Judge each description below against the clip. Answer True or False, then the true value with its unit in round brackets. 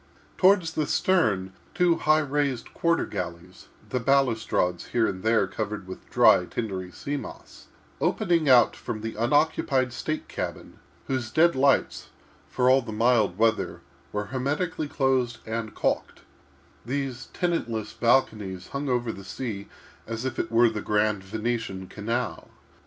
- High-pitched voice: False (120 Hz)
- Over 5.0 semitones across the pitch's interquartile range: False (4.6 semitones)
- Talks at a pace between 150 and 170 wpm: False (135 wpm)